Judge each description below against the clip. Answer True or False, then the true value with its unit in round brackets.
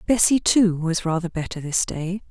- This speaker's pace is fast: False (180 wpm)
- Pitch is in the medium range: True (180 Hz)